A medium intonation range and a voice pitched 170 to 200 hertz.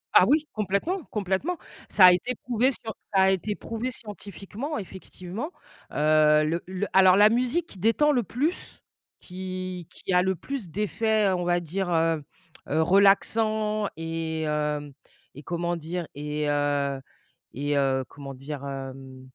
No: wide, 6.0 semitones; medium, 185 Hz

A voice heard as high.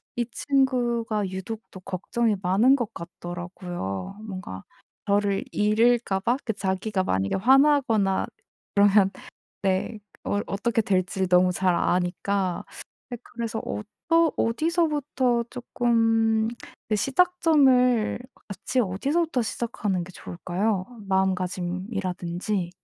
Yes: high, 210 Hz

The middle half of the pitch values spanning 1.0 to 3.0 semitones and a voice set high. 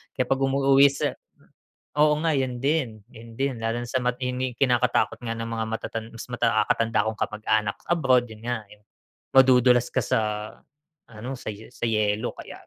No: average, 2.7 semitones; low, 120 Hz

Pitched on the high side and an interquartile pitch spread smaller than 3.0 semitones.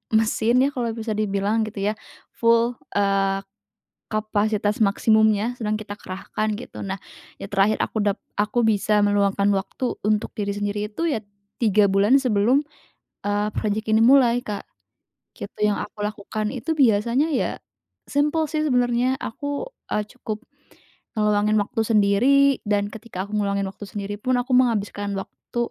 Yes: high, 215 Hz; narrow, 2.6 semitones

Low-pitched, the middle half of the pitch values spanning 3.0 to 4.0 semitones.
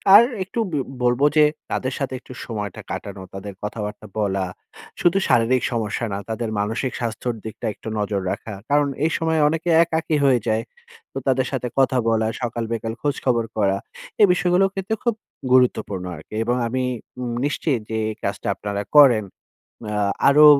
No: low, 120 Hz; average, 4.9 semitones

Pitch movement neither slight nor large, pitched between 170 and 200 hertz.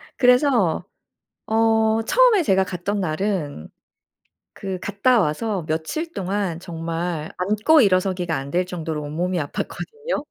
Yes: average, 5.0 semitones; high, 190 Hz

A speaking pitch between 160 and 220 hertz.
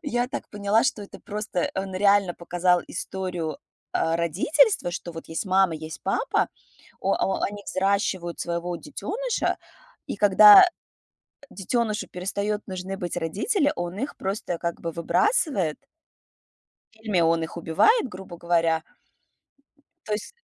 Yes: high, 190 Hz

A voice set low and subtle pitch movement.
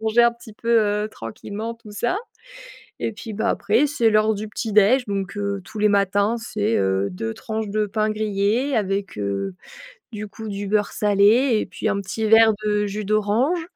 No: high, 215 Hz; narrow, 1.8 semitones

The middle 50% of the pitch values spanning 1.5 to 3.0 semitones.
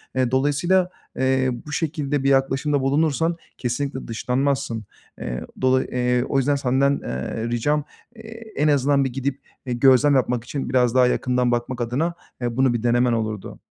Yes: narrow, 2.6 semitones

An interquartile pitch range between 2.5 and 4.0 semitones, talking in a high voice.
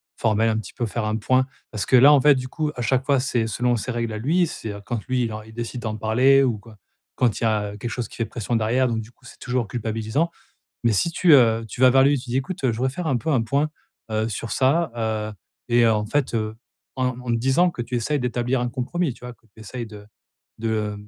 No: average, 2.9 semitones; low, 120 Hz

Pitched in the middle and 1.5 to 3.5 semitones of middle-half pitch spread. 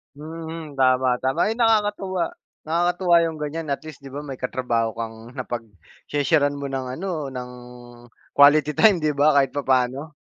No: medium, 145 Hz; average, 4.0 semitones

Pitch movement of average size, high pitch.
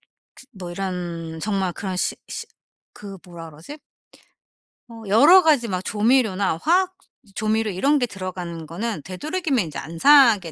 No: wide, 6.8 semitones; high, 200 Hz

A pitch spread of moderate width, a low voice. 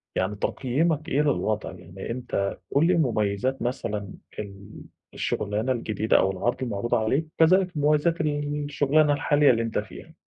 No: wide, 6.0 semitones; low, 130 Hz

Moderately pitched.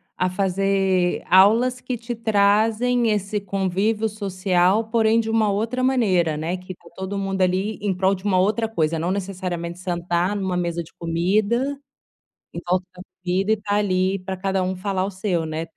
No: high, 195 Hz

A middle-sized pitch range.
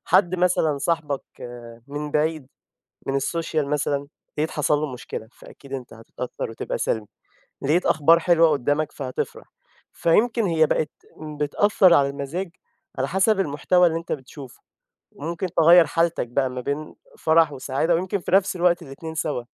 Yes: average, 3.4 semitones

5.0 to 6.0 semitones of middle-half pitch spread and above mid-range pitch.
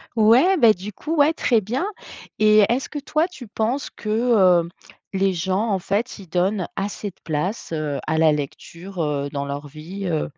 Yes: wide, 5.5 semitones; high, 195 Hz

